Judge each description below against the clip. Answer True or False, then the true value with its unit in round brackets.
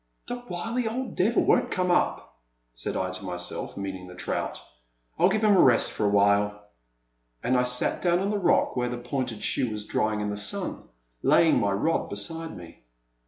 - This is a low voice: True (125 Hz)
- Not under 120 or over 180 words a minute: False (200 wpm)